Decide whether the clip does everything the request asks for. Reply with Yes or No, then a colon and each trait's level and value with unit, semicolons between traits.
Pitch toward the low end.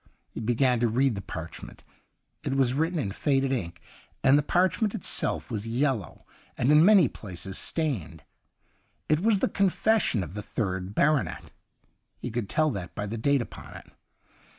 Yes: low, 130 Hz